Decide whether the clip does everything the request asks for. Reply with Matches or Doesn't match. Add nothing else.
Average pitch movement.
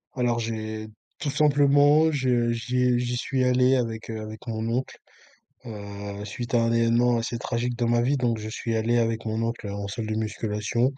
Doesn't match